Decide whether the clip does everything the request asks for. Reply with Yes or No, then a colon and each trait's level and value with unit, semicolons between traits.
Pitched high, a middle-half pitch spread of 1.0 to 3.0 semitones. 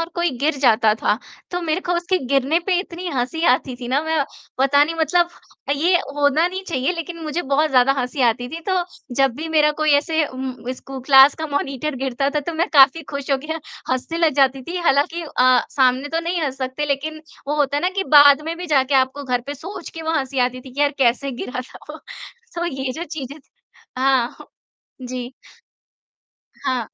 No: very high, 285 Hz; average, 3.7 semitones